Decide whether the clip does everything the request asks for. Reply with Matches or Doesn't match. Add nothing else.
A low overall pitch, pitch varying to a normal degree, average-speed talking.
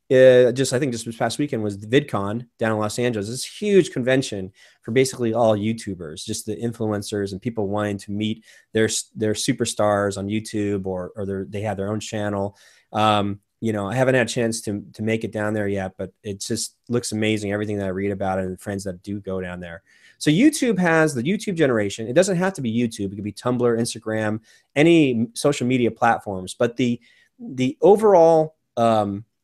Doesn't match